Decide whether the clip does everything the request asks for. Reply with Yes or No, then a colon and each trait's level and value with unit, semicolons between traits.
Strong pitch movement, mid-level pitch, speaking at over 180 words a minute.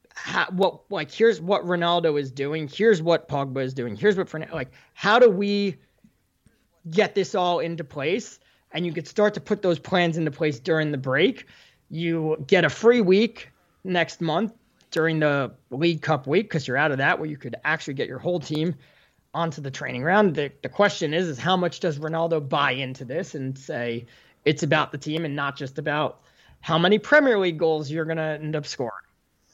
No: average, 3.7 semitones; medium, 160 Hz; average, 200 wpm